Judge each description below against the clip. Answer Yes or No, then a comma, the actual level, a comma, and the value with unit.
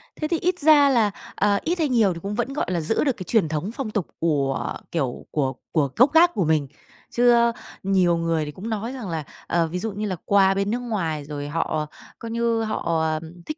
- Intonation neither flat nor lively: No, wide, 6.6 semitones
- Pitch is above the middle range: Yes, high, 200 Hz